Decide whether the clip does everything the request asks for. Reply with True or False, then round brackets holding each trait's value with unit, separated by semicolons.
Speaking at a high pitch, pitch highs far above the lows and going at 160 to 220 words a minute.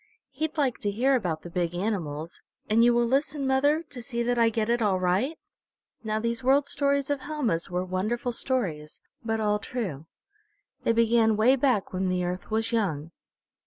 True (230 Hz; 5.9 semitones; 185 wpm)